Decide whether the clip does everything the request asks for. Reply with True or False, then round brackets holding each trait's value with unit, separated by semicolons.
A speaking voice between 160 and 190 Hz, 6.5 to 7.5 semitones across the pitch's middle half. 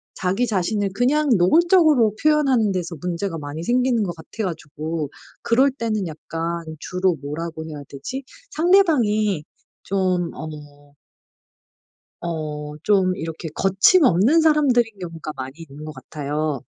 True (185 Hz; 7.2 semitones)